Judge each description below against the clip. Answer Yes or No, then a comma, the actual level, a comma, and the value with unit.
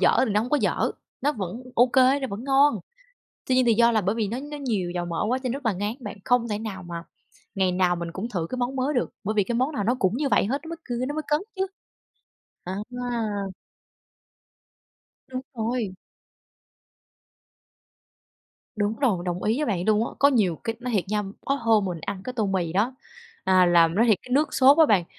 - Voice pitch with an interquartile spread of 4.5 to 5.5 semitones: Yes, average, 5.1 semitones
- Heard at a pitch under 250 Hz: Yes, high, 225 Hz